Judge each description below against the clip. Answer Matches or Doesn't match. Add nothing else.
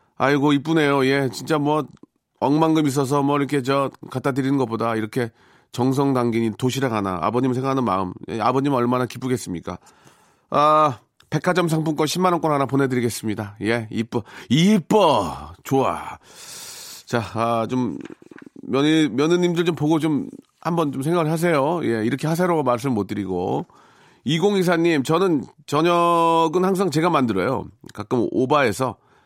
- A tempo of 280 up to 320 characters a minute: Matches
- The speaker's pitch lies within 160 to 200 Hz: Doesn't match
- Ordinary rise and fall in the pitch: Matches